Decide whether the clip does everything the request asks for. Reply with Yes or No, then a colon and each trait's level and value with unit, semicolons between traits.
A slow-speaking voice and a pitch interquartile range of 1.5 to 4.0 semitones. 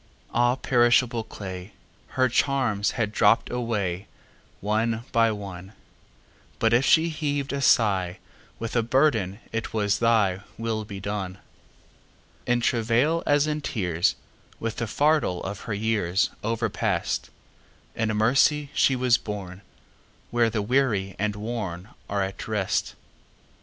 Yes: slow, 100 wpm; average, 3.3 semitones